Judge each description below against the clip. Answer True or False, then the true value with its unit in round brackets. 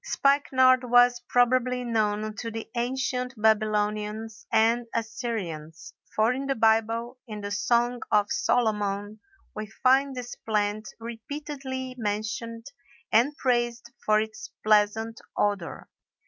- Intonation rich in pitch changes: False (2.7 semitones)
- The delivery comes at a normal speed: False (115 wpm)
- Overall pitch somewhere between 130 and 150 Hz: False (230 Hz)